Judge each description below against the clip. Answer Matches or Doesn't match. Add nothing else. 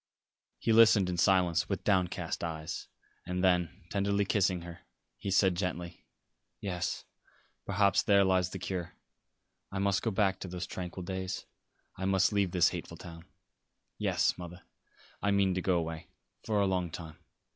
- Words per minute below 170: Matches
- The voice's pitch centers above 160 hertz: Doesn't match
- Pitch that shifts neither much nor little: Doesn't match